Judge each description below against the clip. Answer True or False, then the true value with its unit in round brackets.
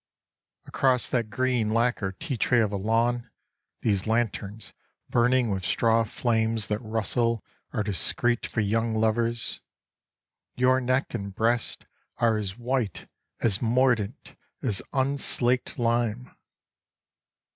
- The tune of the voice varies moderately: False (2.3 semitones)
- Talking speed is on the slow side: True (115 wpm)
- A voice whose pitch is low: True (115 Hz)